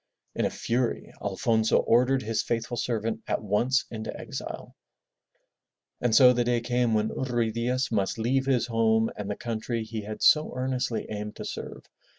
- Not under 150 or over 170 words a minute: Yes, average, 165 wpm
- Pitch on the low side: Yes, low, 115 Hz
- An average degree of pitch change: No, narrow, 2.2 semitones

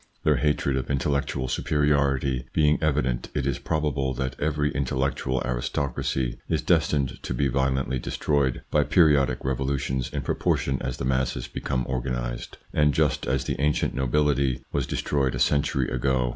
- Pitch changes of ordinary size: No, narrow, 2.0 semitones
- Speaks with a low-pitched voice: Yes, very low, 65 Hz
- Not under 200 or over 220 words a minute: No, average, 155 wpm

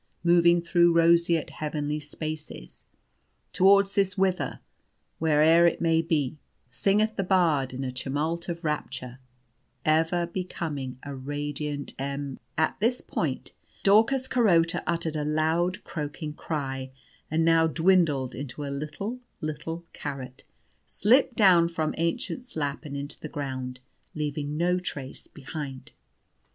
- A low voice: No, medium, 160 Hz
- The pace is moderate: No, slow, 130 wpm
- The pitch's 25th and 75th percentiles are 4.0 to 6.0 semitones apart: No, average, 3.2 semitones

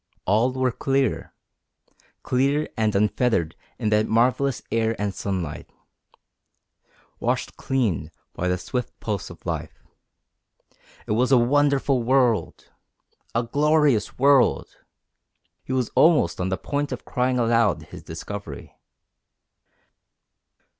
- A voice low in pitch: Yes, low, 120 Hz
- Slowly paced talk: Yes, slow, 115 wpm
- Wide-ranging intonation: No, average, 4.4 semitones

